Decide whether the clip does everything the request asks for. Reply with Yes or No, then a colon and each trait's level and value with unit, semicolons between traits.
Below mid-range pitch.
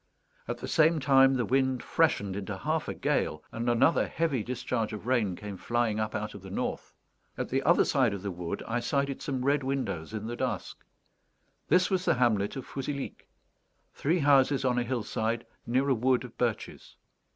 Yes: low, 125 Hz